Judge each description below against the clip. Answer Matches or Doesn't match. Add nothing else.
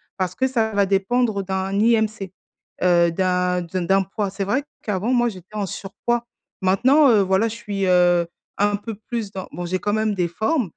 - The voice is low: Doesn't match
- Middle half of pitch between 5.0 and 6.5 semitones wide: Doesn't match